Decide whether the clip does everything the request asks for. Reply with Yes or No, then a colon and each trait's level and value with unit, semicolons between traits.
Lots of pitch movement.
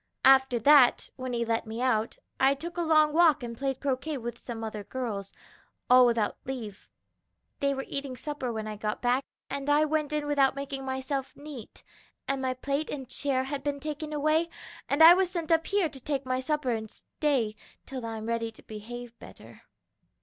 No: average, 3.6 semitones